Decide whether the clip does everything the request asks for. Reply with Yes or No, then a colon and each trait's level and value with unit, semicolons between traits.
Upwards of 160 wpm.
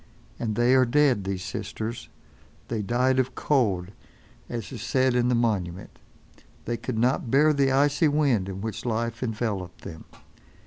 No: average, 155 wpm